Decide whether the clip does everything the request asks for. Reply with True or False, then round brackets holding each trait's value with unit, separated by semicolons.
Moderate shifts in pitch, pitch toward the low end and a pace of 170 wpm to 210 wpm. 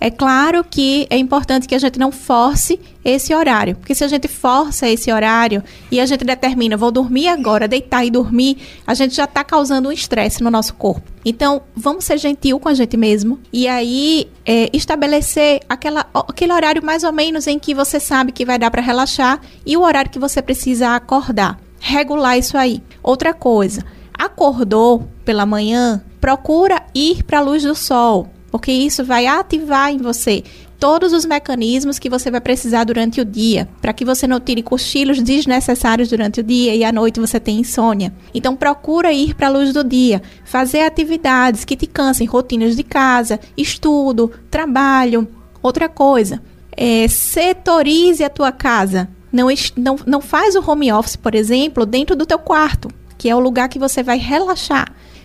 False (3.6 semitones; 260 Hz; 180 wpm)